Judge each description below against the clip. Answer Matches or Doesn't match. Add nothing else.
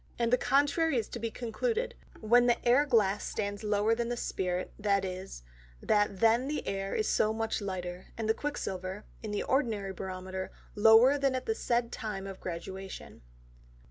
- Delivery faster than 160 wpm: Matches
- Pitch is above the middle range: Matches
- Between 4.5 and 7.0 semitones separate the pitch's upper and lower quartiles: Doesn't match